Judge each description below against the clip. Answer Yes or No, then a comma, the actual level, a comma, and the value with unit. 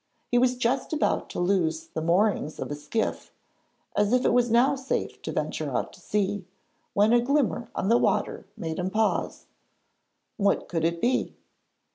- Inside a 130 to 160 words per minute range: No, average, 170 wpm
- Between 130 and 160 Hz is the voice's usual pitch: No, high, 210 Hz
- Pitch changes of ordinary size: No, wide, 5.7 semitones